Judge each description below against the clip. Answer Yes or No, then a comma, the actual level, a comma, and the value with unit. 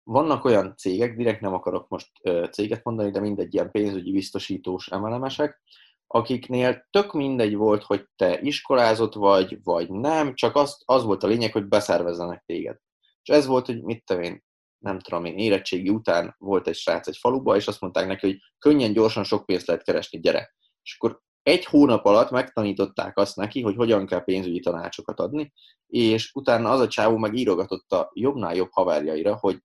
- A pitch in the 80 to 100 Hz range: No, low, 110 Hz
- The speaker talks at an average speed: No, fast, 180 wpm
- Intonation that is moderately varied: Yes, average, 4.5 semitones